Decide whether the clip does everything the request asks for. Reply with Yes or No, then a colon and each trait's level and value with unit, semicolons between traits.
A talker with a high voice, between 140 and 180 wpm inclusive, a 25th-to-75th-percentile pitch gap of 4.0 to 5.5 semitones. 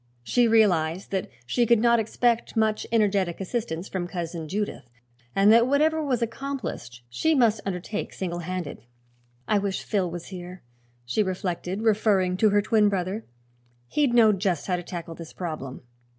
Yes: high, 195 Hz; average, 160 wpm; average, 4.3 semitones